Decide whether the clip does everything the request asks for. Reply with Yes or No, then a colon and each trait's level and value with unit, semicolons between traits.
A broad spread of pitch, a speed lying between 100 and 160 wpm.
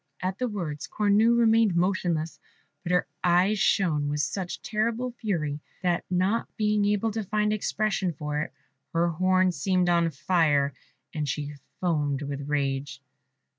Yes: wide, 5.7 semitones; average, 145 wpm